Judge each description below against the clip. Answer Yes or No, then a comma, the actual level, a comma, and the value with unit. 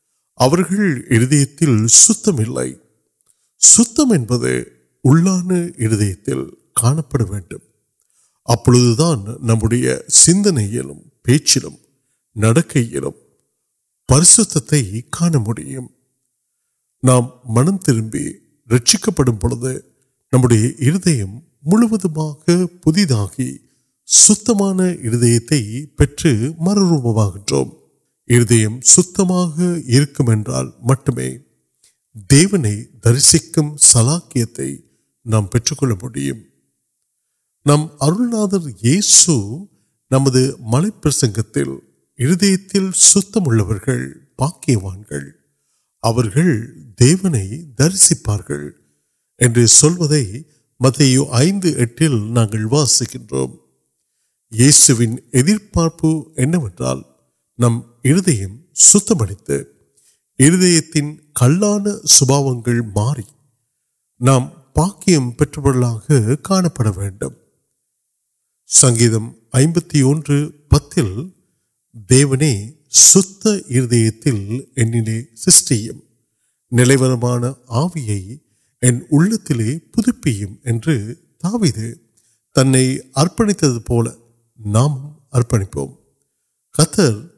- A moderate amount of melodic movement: No, wide, 5.7 semitones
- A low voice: Yes, low, 130 Hz